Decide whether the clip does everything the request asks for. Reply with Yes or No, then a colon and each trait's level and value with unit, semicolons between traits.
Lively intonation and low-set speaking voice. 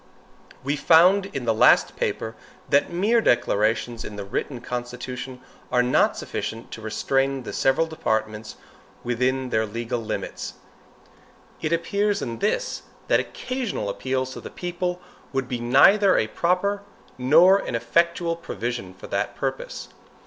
Yes: wide, 6.7 semitones; low, 130 Hz